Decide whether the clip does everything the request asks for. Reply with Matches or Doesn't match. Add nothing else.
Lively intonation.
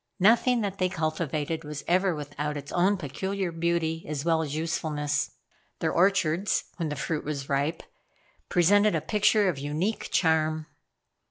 Doesn't match